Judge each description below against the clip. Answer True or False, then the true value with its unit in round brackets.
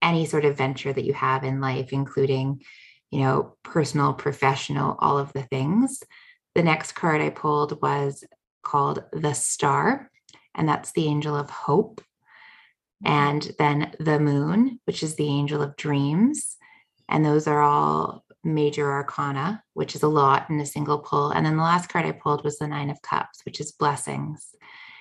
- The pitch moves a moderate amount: False (2.0 semitones)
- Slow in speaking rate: False (175 wpm)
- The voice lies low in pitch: False (145 Hz)